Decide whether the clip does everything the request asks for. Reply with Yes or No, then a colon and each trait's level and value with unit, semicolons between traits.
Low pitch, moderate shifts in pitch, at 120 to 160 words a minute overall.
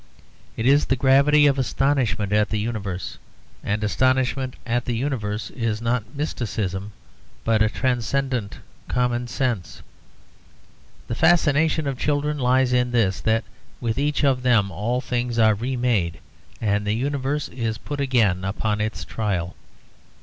Yes: low, 120 Hz; average, 4.0 semitones; average, 140 wpm